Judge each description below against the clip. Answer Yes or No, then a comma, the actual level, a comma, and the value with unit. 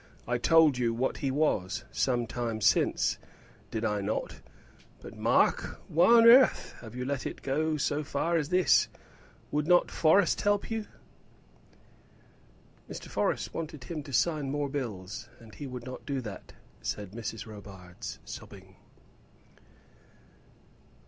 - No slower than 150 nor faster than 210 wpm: No, average, 140 wpm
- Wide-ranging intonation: Yes, wide, 5.7 semitones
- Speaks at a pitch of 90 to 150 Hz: Yes, low, 135 Hz